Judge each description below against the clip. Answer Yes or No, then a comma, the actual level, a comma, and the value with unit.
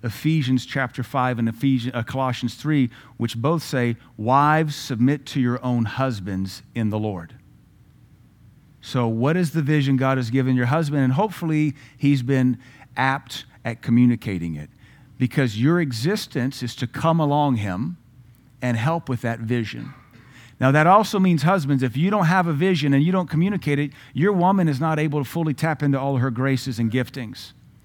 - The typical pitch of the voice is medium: No, low, 130 Hz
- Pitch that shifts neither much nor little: Yes, average, 3.6 semitones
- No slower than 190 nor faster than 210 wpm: No, average, 175 wpm